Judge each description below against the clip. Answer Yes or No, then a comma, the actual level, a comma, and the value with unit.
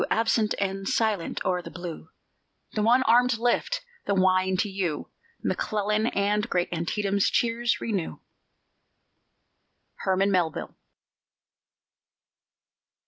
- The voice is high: Yes, high, 200 Hz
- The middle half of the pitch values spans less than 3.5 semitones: Yes, average, 3.1 semitones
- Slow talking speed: Yes, slow, 100 wpm